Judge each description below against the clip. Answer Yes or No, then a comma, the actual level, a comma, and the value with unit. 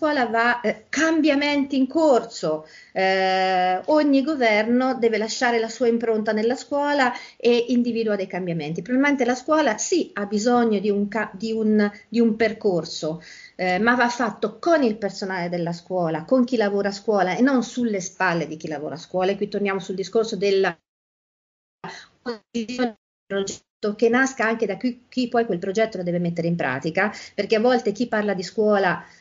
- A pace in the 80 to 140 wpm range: No, fast, 170 wpm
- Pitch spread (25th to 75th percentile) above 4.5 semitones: No, average, 4.2 semitones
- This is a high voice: Yes, high, 220 Hz